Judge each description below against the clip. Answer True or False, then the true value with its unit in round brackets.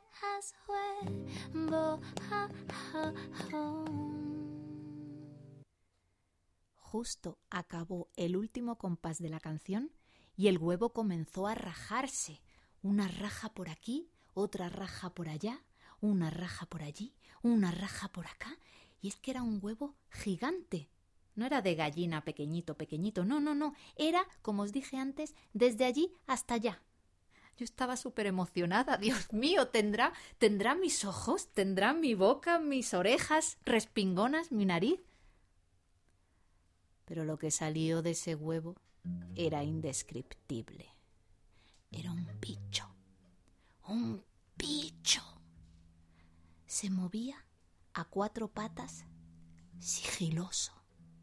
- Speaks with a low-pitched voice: False (185 Hz)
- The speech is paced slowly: True (110 wpm)